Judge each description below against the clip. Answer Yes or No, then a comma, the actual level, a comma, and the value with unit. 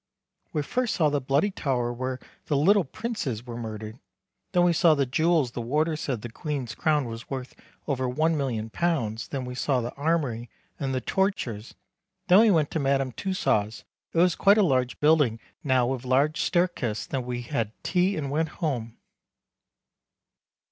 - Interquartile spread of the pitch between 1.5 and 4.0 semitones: No, average, 5.0 semitones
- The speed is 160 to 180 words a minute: Yes, average, 170 wpm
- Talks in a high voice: No, medium, 140 Hz